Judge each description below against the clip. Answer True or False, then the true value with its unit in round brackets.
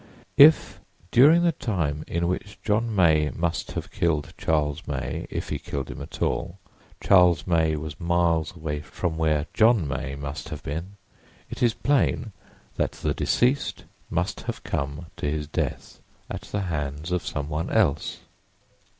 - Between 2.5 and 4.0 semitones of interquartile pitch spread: False (4.4 semitones)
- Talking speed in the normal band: True (155 wpm)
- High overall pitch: False (80 Hz)